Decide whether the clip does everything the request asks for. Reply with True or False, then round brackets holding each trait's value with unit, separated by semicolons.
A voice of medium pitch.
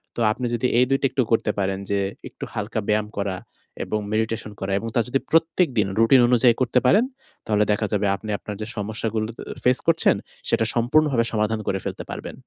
False (115 Hz)